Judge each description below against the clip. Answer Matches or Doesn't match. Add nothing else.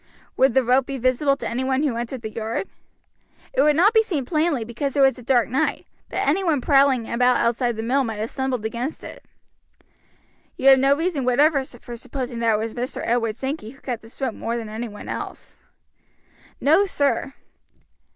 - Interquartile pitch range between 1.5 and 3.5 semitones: Matches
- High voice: Matches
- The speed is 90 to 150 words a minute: Doesn't match